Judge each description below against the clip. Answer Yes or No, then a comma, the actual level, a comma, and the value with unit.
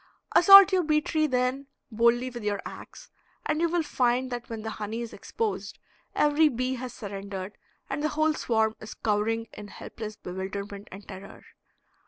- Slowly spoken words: No, average, 170 wpm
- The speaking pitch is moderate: No, high, 240 Hz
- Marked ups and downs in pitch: Yes, wide, 6.2 semitones